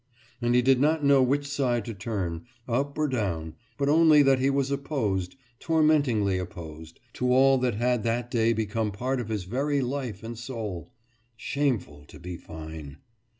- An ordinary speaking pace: Yes, average, 170 wpm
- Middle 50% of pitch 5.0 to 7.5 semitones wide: Yes, wide, 5.5 semitones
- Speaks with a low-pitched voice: Yes, low, 120 Hz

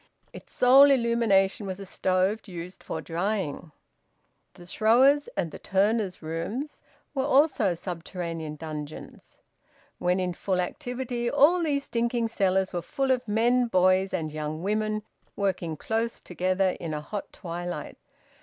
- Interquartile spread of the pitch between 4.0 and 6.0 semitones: Yes, average, 5.1 semitones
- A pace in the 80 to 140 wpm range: Yes, slow, 135 wpm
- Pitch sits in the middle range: No, high, 195 Hz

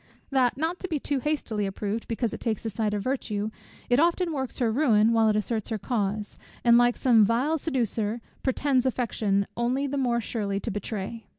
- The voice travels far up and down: No, average, 3.8 semitones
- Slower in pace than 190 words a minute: No, average, 195 wpm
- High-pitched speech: Yes, high, 235 Hz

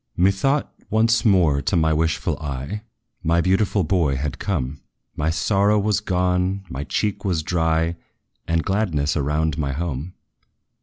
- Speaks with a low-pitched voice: Yes, very low, 85 Hz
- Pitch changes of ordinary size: Yes, average, 4.4 semitones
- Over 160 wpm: No, average, 140 wpm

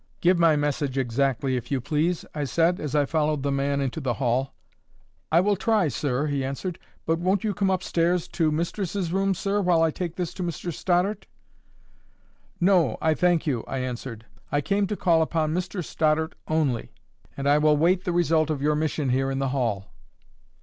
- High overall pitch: No, medium, 155 Hz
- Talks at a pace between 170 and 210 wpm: Yes, average, 195 wpm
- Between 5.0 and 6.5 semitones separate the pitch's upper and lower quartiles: No, average, 4.3 semitones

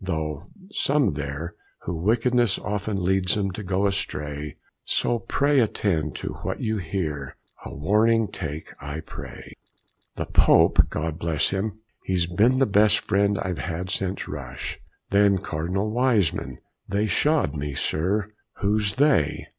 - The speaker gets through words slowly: No, average, 145 wpm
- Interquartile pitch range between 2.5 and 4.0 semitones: No, average, 5.1 semitones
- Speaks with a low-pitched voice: Yes, very low, 95 Hz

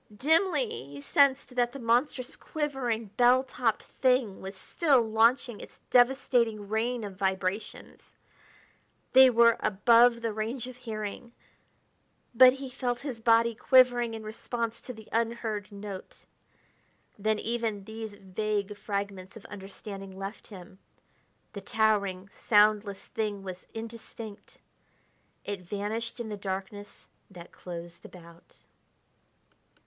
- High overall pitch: Yes, high, 220 Hz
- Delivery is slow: Yes, slow, 120 wpm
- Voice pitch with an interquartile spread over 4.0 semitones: No, average, 3.3 semitones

